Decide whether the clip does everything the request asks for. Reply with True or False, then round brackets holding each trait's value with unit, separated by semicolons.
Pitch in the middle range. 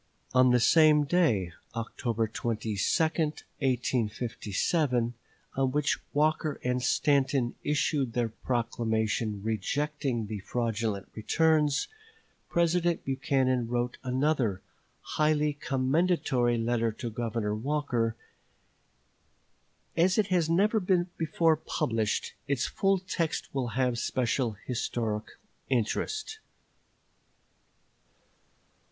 False (130 Hz)